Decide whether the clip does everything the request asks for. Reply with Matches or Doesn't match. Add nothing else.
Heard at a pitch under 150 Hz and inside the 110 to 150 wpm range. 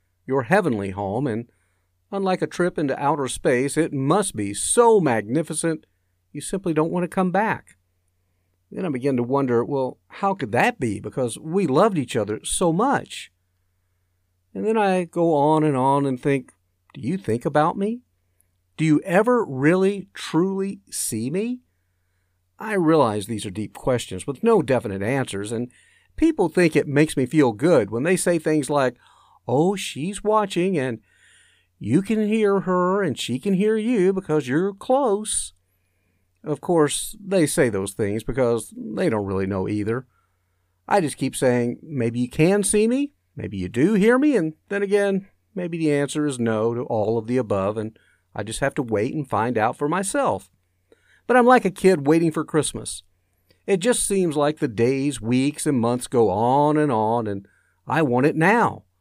Doesn't match